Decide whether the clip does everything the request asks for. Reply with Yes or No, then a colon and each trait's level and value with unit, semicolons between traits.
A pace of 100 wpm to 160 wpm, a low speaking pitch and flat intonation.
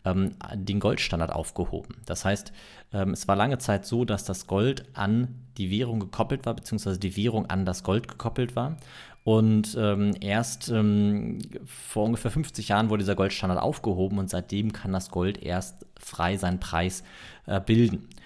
No: average, 150 wpm; low, 105 Hz; average, 3.2 semitones